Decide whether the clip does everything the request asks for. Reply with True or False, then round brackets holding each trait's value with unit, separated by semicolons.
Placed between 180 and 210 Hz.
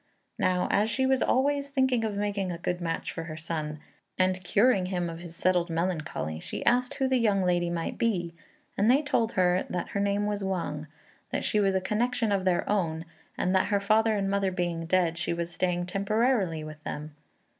True (185 Hz)